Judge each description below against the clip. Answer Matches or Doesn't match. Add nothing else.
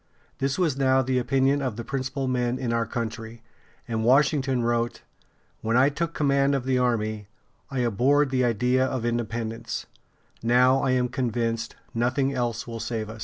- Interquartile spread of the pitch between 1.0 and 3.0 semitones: Matches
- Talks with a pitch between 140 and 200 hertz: Doesn't match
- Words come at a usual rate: Matches